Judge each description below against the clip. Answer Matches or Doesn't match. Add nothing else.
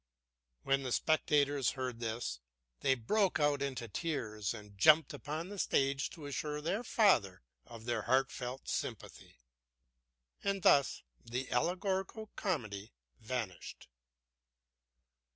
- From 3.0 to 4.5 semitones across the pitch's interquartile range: Doesn't match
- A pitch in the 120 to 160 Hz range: Matches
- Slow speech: Matches